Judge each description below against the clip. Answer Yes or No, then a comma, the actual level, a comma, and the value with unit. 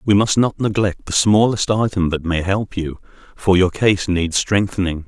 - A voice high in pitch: No, very low, 95 Hz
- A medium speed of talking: Yes, average, 190 wpm